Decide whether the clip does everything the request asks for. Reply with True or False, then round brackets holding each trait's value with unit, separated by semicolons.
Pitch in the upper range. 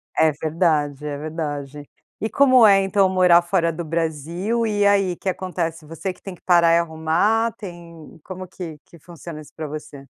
False (170 Hz)